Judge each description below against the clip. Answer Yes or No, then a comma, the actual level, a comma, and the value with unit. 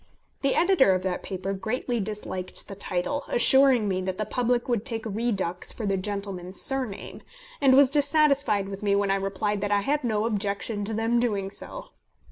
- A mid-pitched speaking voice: No, high, 210 Hz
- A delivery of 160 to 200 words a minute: Yes, average, 185 wpm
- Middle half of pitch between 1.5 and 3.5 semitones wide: No, average, 4.1 semitones